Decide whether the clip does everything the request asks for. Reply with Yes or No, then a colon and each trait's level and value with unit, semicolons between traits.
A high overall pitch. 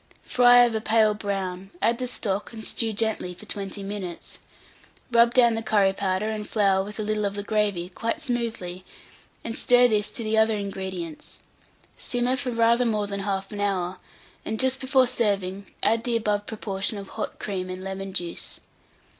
Yes: high, 210 Hz